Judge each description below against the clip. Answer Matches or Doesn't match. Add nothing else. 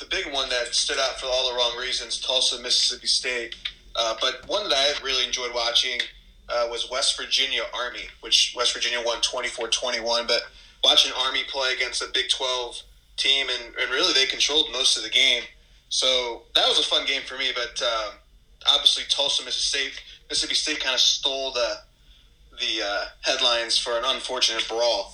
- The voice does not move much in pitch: Matches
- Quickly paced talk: Doesn't match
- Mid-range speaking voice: Doesn't match